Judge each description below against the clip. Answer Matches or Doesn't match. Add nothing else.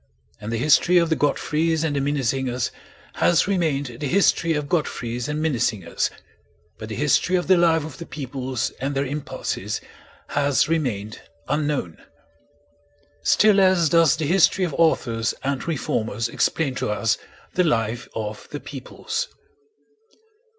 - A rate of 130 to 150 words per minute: Matches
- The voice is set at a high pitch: Doesn't match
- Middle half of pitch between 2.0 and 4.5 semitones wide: Doesn't match